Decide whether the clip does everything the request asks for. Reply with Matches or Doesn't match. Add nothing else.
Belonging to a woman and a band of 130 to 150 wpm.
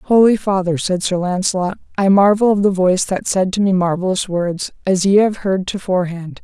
Doesn't match